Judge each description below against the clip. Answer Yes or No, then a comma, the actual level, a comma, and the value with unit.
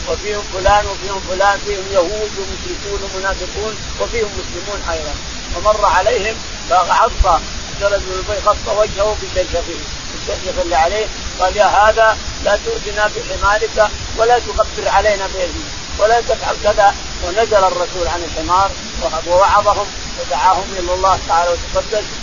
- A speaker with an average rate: Yes, average, 115 wpm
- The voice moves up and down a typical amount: No, narrow, 2.2 semitones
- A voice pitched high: Yes, high, 200 Hz